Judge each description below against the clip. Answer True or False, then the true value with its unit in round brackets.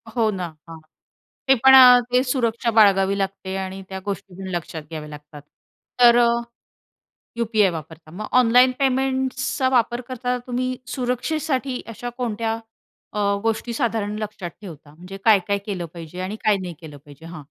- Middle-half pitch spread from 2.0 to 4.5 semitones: False (5.6 semitones)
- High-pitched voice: True (215 Hz)